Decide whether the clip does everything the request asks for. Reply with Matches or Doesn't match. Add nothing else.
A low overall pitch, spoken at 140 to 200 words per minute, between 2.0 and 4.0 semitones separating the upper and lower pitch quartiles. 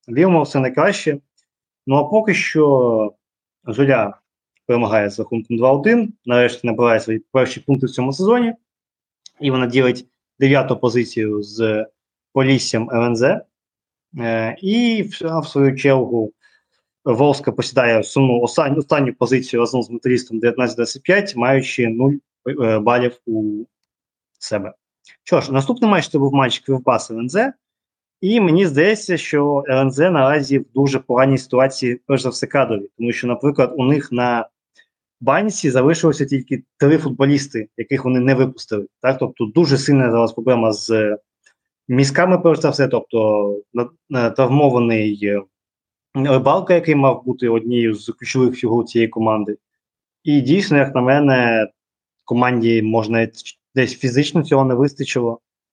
Doesn't match